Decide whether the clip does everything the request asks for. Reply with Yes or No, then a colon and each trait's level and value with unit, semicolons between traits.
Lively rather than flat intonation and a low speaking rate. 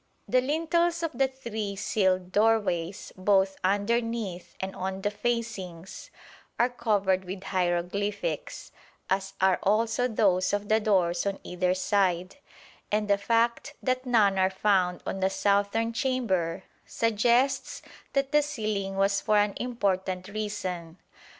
No: average, 3.6 semitones; slow, 130 wpm